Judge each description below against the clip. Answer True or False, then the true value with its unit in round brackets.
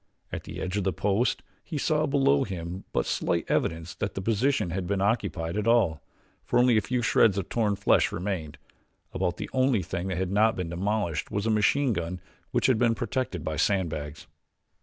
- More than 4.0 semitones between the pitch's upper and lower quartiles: True (4.7 semitones)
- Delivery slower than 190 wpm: False (200 wpm)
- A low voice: True (100 Hz)